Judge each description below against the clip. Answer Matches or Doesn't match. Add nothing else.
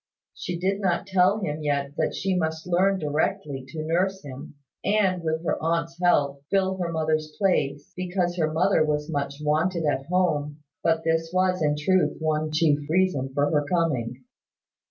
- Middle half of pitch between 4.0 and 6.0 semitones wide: Doesn't match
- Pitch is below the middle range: Doesn't match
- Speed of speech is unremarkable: Matches